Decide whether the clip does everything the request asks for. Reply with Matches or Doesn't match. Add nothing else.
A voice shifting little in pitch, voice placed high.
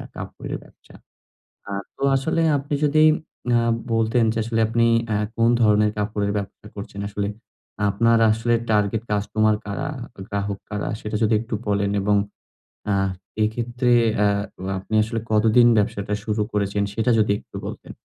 Doesn't match